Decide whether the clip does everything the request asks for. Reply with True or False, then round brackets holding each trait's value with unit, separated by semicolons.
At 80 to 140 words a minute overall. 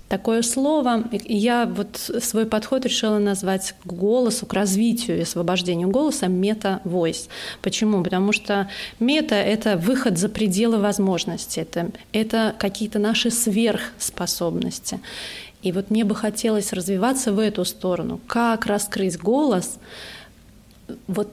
True (125 wpm)